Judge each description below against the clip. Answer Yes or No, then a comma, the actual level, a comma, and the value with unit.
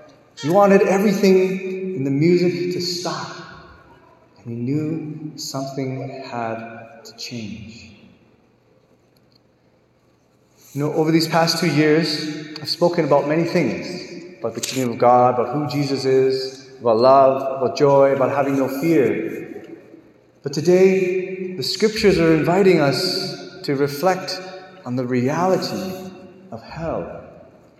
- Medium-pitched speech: Yes, medium, 155 Hz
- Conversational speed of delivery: No, slow, 125 wpm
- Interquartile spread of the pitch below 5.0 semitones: No, wide, 5.4 semitones